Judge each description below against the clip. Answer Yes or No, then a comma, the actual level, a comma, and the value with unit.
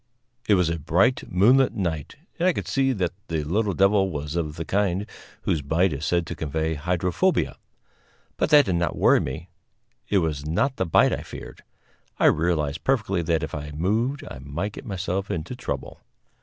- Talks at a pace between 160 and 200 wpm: Yes, average, 185 wpm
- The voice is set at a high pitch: No, very low, 90 Hz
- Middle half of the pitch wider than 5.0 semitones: No, average, 4.5 semitones